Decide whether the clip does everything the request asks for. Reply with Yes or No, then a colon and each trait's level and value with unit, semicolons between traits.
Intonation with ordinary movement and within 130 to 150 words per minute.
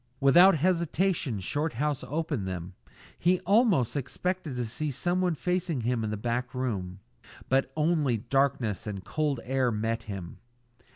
No: wide, 6.4 semitones; slow, 135 wpm